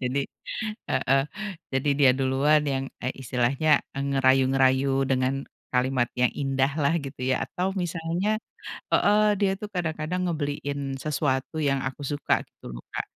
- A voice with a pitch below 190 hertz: Yes, medium, 140 Hz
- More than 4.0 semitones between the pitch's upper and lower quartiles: No, average, 3.0 semitones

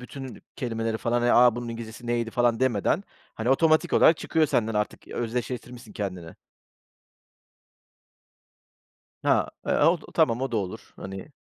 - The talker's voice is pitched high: No, low, 120 Hz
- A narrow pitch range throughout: Yes, narrow, 2.3 semitones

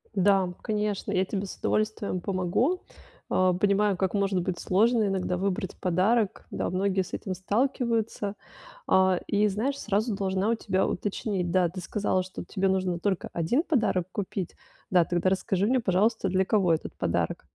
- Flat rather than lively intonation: Yes, narrow, 2.3 semitones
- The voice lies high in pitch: Yes, high, 195 Hz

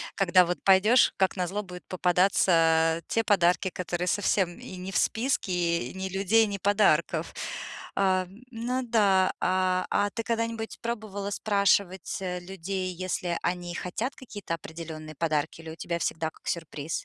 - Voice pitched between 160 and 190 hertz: Yes, medium, 185 Hz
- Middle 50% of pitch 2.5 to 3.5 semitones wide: Yes, average, 2.8 semitones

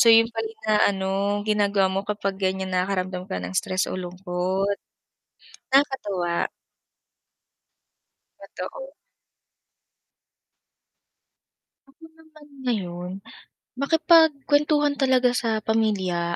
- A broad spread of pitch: Yes, wide, 6.2 semitones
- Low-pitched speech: No, high, 205 Hz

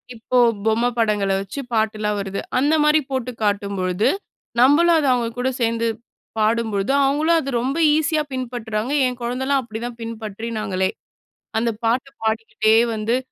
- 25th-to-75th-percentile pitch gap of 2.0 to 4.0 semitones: Yes, average, 3.3 semitones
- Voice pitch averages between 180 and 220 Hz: No, high, 230 Hz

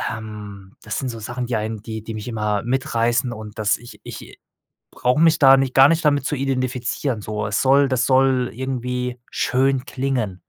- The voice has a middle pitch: No, low, 125 Hz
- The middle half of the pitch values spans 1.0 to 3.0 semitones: No, average, 3.4 semitones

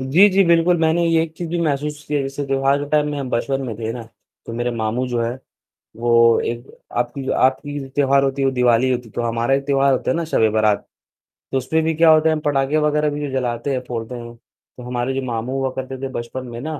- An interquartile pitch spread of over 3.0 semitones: Yes, average, 3.6 semitones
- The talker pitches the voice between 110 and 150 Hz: Yes, low, 135 Hz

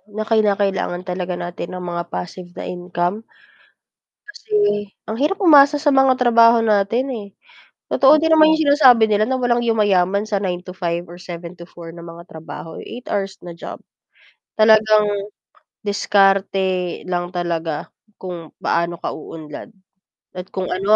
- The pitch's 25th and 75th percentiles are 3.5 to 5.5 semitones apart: Yes, average, 4.7 semitones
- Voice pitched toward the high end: Yes, high, 195 Hz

